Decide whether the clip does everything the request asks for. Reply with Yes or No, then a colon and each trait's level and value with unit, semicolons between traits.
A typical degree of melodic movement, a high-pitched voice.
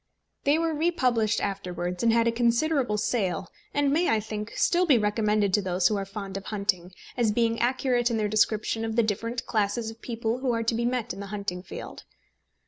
Yes: average, 3.0 semitones; high, 225 Hz